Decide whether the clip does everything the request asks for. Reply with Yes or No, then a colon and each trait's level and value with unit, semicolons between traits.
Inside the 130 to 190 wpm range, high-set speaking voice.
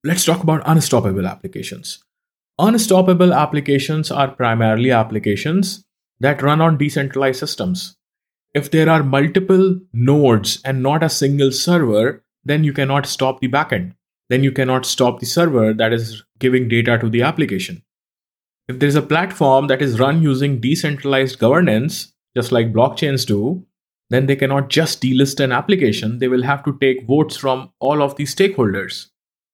No: average, 155 wpm; medium, 140 Hz